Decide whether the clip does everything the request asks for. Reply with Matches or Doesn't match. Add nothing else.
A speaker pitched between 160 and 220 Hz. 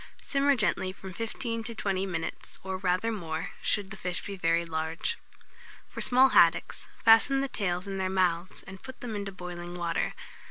Matches